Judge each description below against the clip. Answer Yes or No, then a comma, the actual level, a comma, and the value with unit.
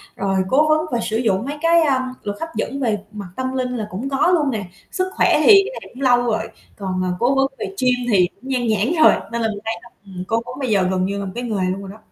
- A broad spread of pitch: No, average, 4.9 semitones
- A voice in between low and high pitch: No, high, 240 Hz